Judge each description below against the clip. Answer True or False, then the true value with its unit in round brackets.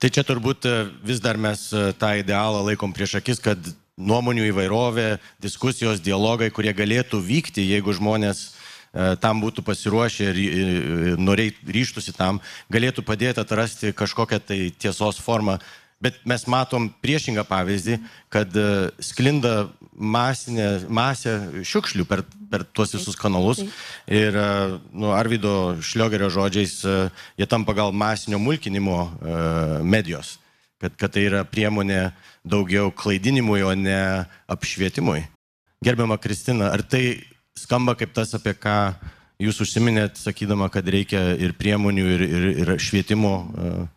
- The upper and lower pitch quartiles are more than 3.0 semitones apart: False (2.7 semitones)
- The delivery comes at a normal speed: False (125 wpm)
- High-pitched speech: False (105 Hz)